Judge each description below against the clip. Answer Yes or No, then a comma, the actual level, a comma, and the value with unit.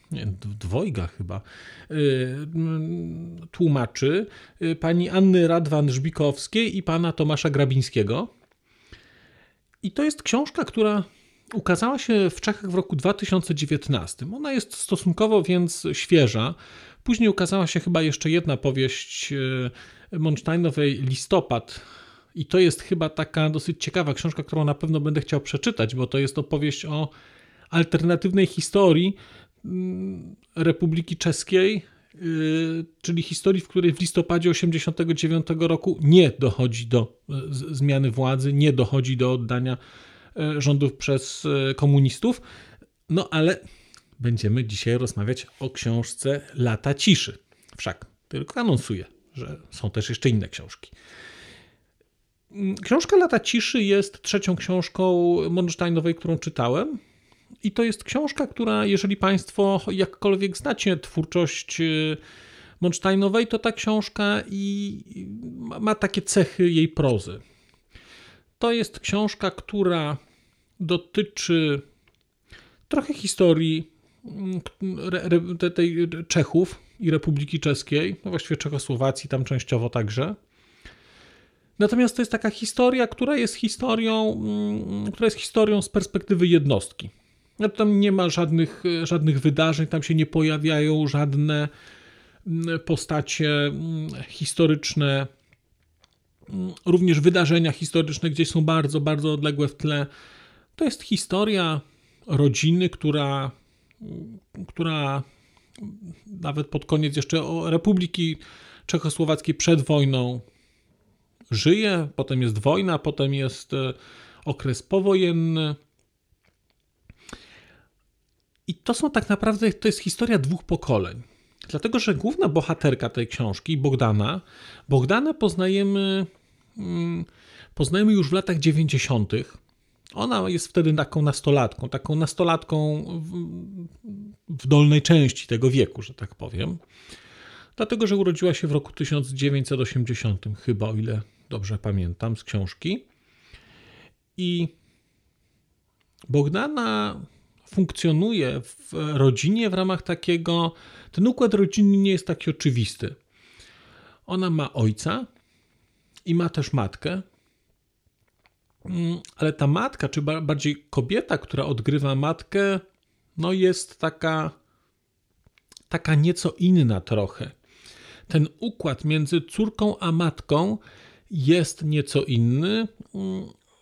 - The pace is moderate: No, slow, 105 wpm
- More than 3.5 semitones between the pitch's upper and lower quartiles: Yes, average, 5.3 semitones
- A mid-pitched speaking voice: Yes, medium, 160 Hz